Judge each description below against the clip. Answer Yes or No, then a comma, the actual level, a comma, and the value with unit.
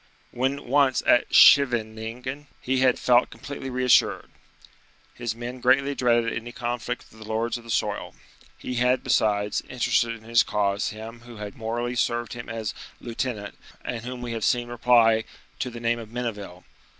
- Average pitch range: No, narrow, 1.8 semitones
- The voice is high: No, low, 120 Hz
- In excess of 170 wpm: No, average, 165 wpm